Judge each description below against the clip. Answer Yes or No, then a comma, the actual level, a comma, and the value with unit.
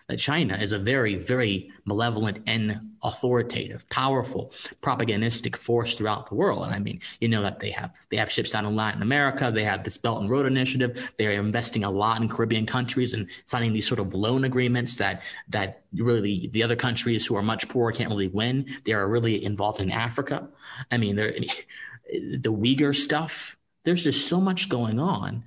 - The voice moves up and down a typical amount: Yes, average, 3.0 semitones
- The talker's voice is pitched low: Yes, low, 115 Hz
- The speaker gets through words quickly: No, average, 190 wpm